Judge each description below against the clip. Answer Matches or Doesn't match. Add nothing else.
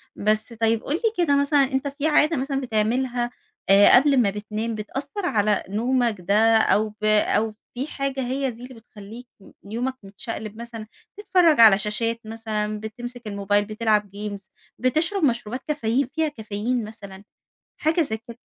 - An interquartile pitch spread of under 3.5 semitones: Doesn't match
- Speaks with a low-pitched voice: Doesn't match